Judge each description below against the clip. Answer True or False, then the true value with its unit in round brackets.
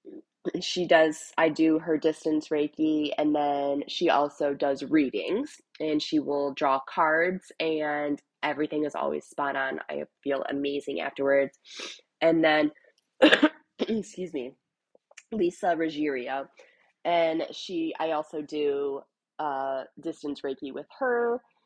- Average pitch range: True (3.1 semitones)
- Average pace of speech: False (120 wpm)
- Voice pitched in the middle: True (155 Hz)